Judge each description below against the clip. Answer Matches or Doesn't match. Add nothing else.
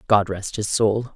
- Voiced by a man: Doesn't match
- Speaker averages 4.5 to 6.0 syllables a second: Doesn't match